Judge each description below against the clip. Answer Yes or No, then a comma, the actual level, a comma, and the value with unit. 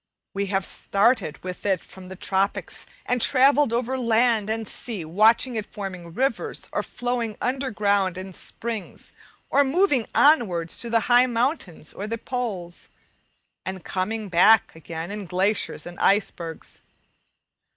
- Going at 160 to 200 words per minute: No, average, 140 wpm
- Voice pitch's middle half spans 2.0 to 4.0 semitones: No, average, 4.5 semitones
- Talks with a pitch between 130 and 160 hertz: No, high, 210 Hz